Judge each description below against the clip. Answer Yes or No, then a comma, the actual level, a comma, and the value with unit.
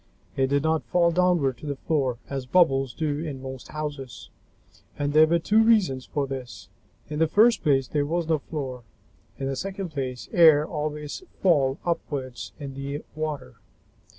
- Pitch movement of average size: Yes, average, 3.3 semitones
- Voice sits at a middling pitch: Yes, medium, 145 Hz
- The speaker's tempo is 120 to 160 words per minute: No, average, 170 wpm